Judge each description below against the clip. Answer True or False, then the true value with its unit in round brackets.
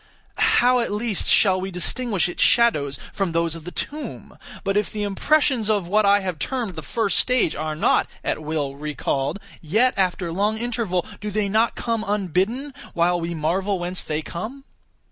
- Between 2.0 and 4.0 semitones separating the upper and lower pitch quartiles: False (4.8 semitones)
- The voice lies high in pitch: True (195 Hz)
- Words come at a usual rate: True (180 wpm)